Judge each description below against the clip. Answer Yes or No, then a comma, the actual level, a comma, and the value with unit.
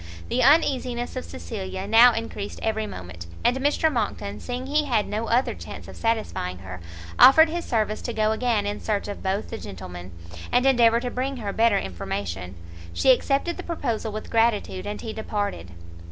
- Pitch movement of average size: Yes, average, 3.8 semitones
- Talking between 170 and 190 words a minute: Yes, average, 180 wpm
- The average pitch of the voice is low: No, high, 225 Hz